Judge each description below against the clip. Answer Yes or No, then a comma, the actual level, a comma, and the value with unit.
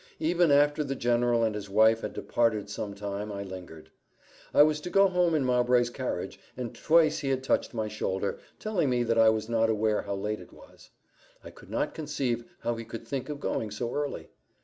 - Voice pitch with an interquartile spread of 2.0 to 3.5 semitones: No, average, 5.0 semitones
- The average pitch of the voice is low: Yes, low, 120 Hz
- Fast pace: Yes, fast, 210 wpm